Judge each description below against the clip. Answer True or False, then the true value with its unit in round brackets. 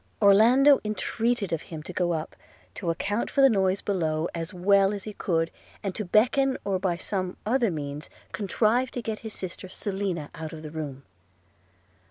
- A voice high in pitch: True (195 Hz)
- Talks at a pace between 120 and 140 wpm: False (180 wpm)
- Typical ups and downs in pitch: True (4.5 semitones)